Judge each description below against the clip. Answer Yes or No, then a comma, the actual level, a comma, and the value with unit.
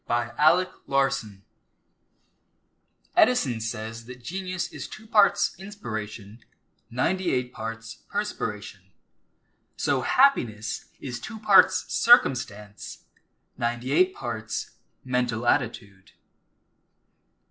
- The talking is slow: Yes, slow, 90 wpm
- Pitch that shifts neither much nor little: No, wide, 8.6 semitones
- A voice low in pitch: Yes, low, 125 Hz